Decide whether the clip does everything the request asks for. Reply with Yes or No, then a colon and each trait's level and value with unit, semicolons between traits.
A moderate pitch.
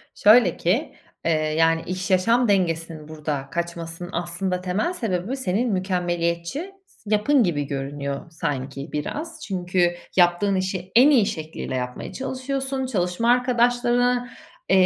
Yes: medium, 180 Hz